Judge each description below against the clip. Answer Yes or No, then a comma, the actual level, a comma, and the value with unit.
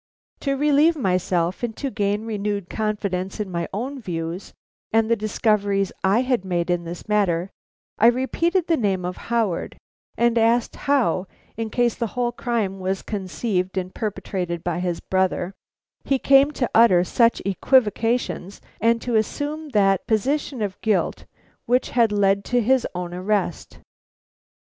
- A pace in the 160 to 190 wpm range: No, average, 150 wpm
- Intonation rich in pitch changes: No, average, 4.3 semitones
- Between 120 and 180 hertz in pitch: No, high, 210 Hz